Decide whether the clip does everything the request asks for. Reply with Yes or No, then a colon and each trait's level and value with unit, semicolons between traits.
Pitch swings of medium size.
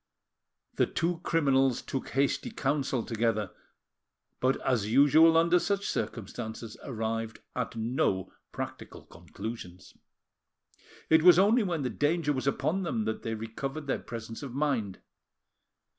No: wide, 5.8 semitones